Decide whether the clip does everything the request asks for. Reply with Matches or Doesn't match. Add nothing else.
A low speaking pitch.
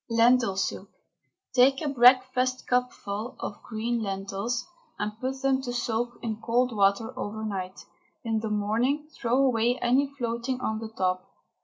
Doesn't match